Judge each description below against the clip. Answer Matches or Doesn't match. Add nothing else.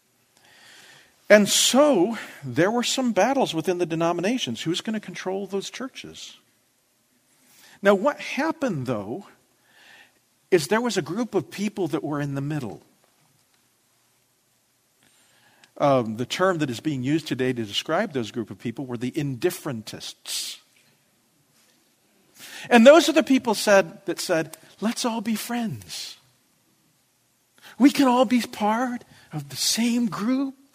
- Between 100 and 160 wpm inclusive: Matches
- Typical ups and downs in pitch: Doesn't match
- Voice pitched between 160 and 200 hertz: Matches